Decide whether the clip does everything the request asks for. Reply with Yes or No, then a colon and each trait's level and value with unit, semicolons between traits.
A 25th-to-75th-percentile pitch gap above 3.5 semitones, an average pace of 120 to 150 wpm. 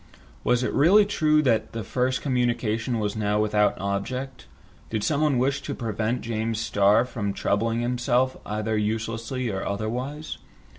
No: average, 3.2 semitones; average, 145 wpm